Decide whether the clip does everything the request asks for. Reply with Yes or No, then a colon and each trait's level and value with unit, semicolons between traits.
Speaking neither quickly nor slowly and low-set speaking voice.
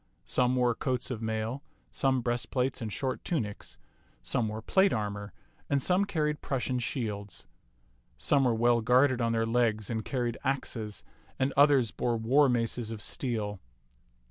Yes: average, 150 wpm; low, 120 Hz